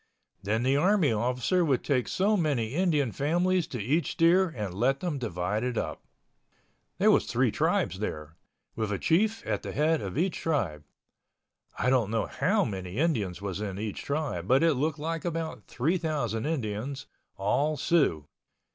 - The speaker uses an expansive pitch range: Yes, wide, 7.4 semitones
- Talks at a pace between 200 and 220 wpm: No, average, 165 wpm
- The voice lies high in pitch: No, low, 135 Hz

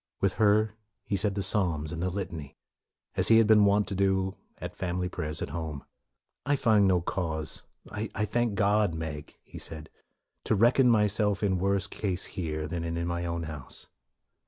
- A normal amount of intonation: Yes, average, 3.9 semitones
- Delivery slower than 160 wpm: No, average, 185 wpm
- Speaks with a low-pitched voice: Yes, very low, 95 Hz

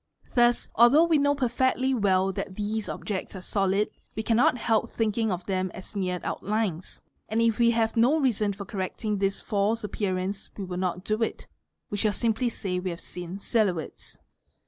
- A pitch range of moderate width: Yes, average, 3.4 semitones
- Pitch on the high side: Yes, high, 210 Hz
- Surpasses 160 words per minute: Yes, average, 185 wpm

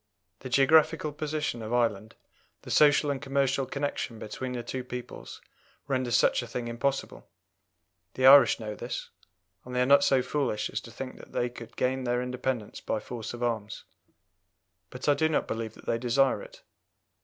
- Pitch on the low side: Yes, low, 125 Hz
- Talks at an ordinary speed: Yes, average, 180 wpm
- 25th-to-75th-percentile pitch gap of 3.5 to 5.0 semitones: No, average, 2.8 semitones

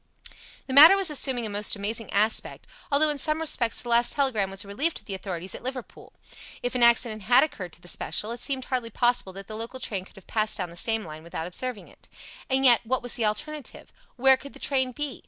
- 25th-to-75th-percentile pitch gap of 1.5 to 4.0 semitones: No, average, 4.5 semitones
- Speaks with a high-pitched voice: Yes, high, 235 Hz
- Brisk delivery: Yes, fast, 235 wpm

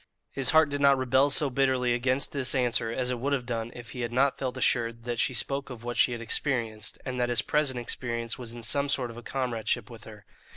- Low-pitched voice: Yes, low, 125 Hz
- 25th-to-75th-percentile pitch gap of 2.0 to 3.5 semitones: Yes, narrow, 2.4 semitones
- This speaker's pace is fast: Yes, fast, 240 wpm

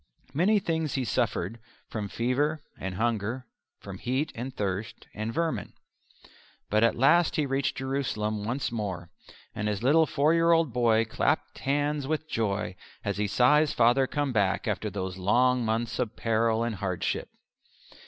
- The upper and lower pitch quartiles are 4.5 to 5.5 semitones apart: Yes, average, 5.0 semitones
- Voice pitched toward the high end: No, low, 120 Hz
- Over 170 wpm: No, average, 160 wpm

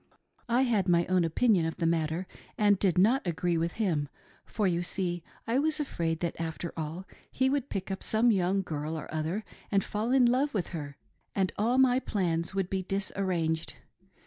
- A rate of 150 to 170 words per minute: No, average, 190 wpm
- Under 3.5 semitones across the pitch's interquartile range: No, average, 4.7 semitones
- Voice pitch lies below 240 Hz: Yes, medium, 185 Hz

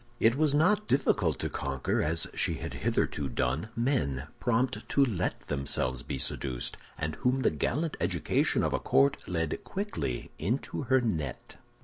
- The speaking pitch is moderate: No, very low, 90 Hz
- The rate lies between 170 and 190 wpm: No, average, 155 wpm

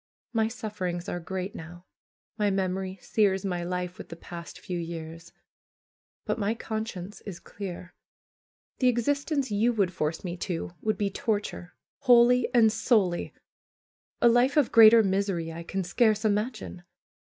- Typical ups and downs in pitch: Yes, average, 4.1 semitones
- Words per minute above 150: No, average, 145 wpm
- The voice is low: No, high, 200 Hz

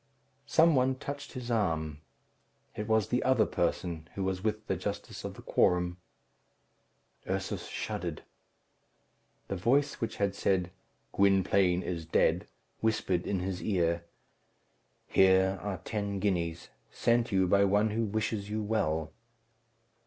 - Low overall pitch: Yes, low, 100 Hz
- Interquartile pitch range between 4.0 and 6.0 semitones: No, average, 3.5 semitones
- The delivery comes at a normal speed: No, slow, 130 wpm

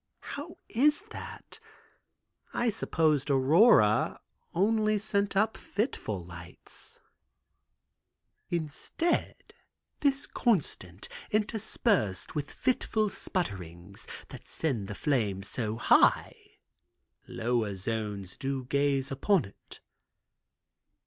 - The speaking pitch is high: No, medium, 140 Hz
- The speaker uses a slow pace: Yes, slow, 85 wpm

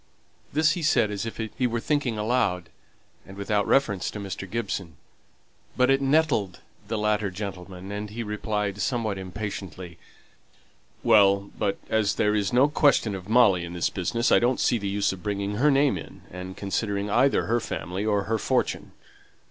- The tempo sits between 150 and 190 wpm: Yes, average, 165 wpm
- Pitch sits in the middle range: No, low, 105 Hz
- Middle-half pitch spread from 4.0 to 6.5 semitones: No, average, 3.2 semitones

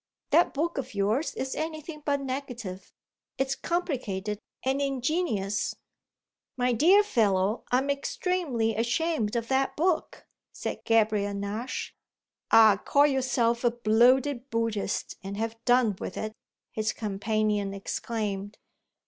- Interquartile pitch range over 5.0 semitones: No, average, 4.6 semitones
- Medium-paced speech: No, slow, 120 wpm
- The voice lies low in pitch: No, high, 235 Hz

